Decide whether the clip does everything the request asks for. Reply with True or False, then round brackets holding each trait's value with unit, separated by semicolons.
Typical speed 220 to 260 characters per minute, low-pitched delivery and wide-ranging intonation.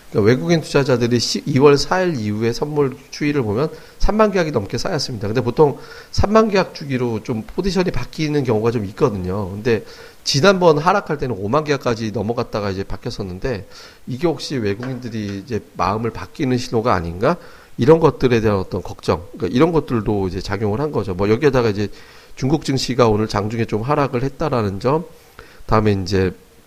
False (370 characters per minute; 125 Hz; 5.9 semitones)